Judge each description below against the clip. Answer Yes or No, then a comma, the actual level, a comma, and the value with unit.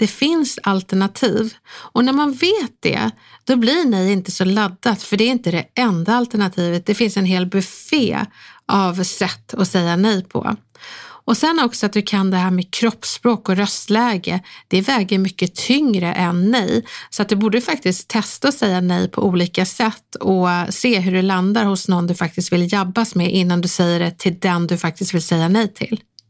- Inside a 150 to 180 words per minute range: No, average, 195 wpm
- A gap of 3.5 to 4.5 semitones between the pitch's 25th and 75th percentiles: Yes, average, 4.0 semitones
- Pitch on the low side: No, high, 195 Hz